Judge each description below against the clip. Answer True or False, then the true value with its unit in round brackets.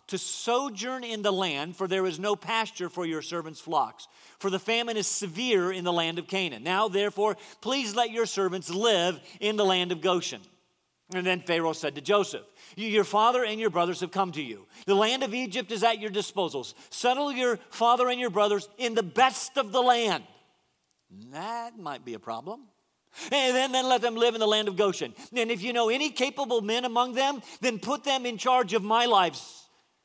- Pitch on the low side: False (215 Hz)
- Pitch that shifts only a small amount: False (4.8 semitones)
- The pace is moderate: False (210 wpm)